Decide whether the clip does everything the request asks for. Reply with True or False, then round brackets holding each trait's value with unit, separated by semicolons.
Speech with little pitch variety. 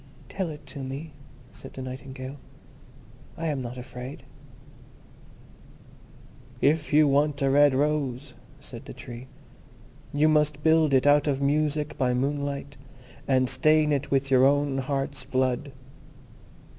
True (2.1 semitones)